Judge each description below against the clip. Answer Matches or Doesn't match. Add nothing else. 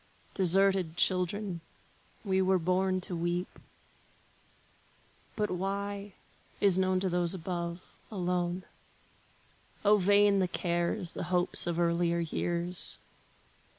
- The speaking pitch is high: Doesn't match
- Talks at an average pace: Doesn't match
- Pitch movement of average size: Doesn't match